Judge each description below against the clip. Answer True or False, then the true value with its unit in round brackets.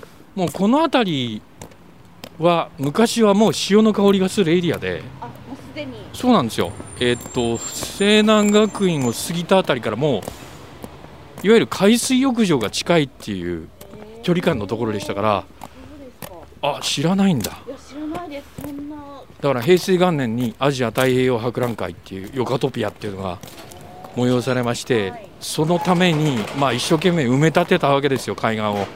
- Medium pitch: True (155 Hz)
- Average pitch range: False (8.5 semitones)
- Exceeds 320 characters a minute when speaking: False (295 characters per minute)